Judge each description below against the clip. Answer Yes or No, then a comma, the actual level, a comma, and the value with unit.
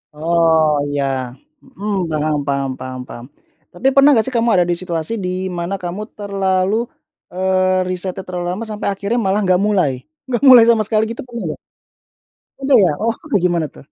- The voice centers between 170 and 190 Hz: Yes, medium, 185 Hz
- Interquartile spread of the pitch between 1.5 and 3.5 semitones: No, average, 4.0 semitones